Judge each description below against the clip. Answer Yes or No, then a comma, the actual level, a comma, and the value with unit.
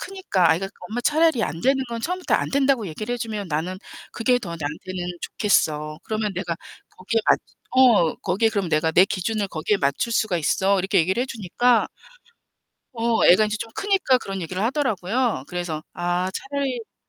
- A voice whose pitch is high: Yes, high, 205 Hz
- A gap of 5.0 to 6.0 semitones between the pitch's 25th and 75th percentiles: Yes, wide, 5.5 semitones